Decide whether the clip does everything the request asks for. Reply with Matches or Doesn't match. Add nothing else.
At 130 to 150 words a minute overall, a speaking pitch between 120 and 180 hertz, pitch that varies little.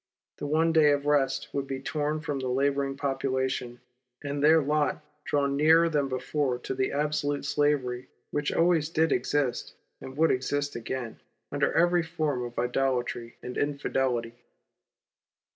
Matches